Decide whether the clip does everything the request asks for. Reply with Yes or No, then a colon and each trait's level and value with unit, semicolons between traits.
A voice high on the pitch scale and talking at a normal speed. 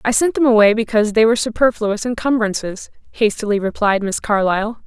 Yes: high, 220 Hz; average, 160 wpm